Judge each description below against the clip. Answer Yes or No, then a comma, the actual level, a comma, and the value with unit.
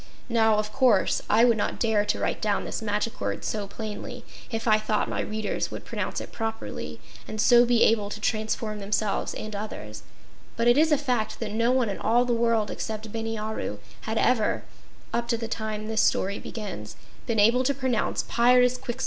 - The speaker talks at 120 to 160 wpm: No, average, 195 wpm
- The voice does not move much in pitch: Yes, narrow, 1.9 semitones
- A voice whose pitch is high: Yes, high, 220 Hz